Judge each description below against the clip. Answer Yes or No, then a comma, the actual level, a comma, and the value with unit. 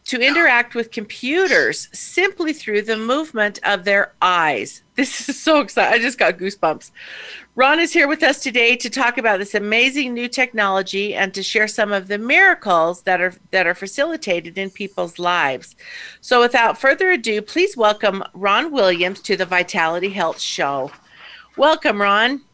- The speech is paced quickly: No, average, 165 wpm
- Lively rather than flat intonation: Yes, wide, 6.1 semitones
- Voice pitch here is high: Yes, high, 220 Hz